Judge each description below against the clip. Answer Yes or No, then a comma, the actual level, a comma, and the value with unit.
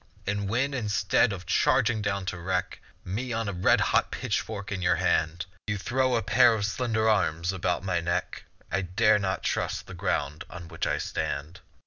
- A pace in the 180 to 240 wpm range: Yes, average, 185 wpm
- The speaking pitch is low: Yes, low, 100 Hz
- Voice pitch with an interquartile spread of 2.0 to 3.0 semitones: No, average, 3.8 semitones